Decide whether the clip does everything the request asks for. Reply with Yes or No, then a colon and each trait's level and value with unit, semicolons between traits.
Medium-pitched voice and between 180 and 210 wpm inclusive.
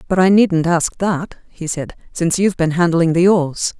Yes: medium, 175 Hz; fast, 205 wpm